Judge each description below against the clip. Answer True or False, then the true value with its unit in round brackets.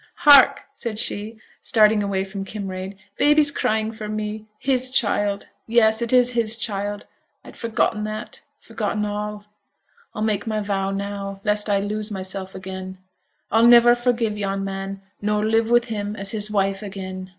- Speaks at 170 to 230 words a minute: False (160 wpm)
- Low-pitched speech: False (210 Hz)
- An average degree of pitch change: False (2.2 semitones)